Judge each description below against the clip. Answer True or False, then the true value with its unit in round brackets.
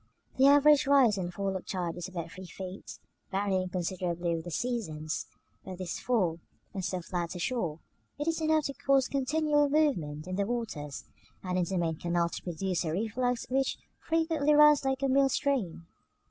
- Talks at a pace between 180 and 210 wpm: True (190 wpm)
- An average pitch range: False (7.9 semitones)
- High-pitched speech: True (195 Hz)